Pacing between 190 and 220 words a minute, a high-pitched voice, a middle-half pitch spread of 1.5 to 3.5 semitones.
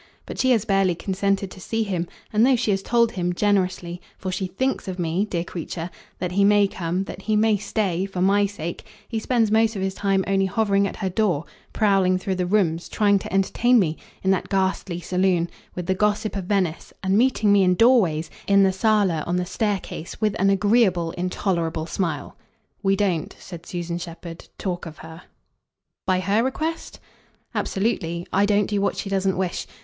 Yes: average, 195 wpm; high, 195 Hz; narrow, 2.6 semitones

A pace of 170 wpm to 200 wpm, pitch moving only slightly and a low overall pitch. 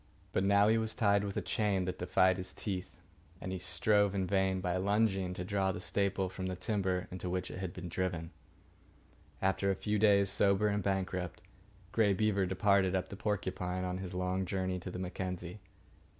Yes: average, 190 wpm; narrow, 1.6 semitones; very low, 95 Hz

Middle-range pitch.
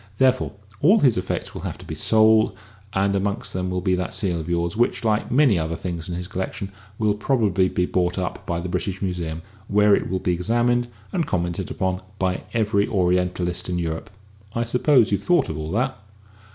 No: very low, 95 Hz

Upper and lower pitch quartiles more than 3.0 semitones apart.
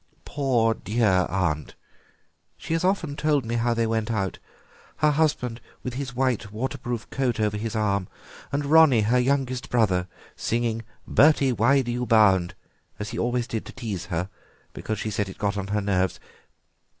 Yes: average, 4.0 semitones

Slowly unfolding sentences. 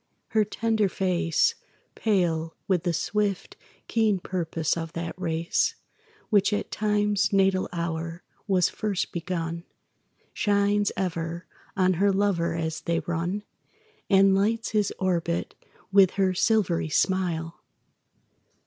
Yes: slow, 115 wpm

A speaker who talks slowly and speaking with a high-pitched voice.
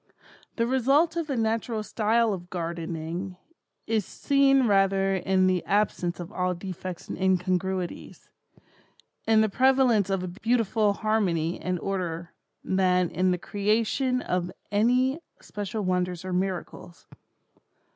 Yes: slow, 125 wpm; high, 195 Hz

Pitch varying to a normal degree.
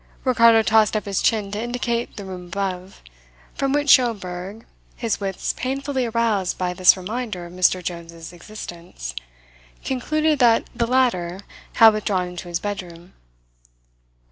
Yes: average, 4.7 semitones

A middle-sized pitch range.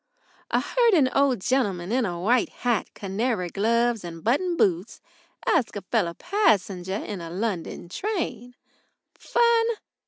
No: wide, 6.0 semitones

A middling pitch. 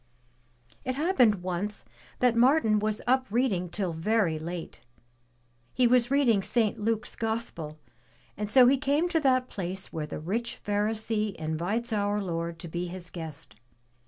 No: high, 210 Hz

